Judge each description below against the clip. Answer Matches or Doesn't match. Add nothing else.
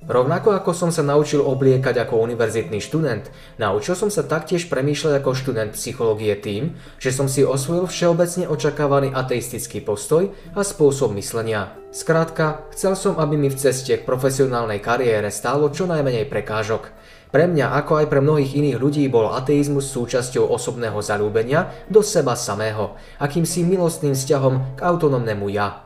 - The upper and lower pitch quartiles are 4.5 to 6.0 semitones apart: Matches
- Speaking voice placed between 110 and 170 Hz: Matches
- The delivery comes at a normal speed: Matches